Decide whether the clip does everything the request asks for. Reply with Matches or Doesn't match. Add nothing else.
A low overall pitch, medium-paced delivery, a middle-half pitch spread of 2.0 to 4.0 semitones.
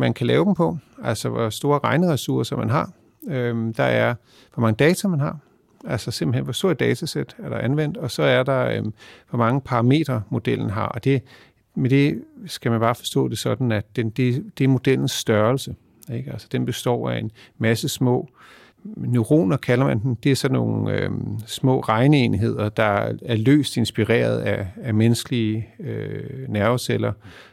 Matches